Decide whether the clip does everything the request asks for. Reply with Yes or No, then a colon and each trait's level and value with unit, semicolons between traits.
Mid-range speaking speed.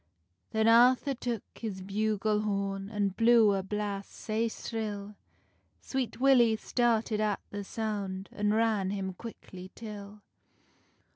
No: slow, 125 wpm